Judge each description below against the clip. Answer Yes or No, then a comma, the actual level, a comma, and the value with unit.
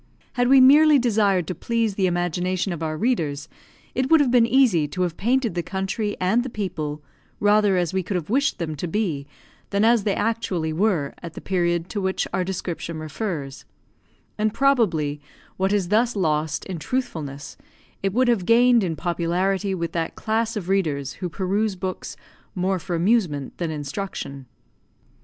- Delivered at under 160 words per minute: No, average, 175 wpm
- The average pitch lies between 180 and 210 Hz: Yes, high, 190 Hz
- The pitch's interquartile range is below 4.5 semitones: No, average, 4.9 semitones